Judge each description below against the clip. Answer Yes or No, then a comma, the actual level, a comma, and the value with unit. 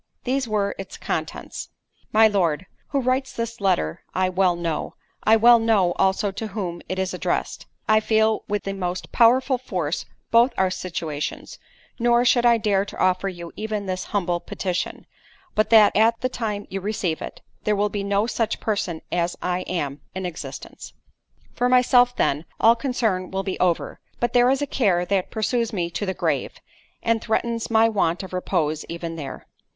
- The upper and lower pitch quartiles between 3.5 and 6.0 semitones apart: Yes, average, 4.0 semitones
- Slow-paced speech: No, average, 175 wpm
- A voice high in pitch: Yes, high, 200 Hz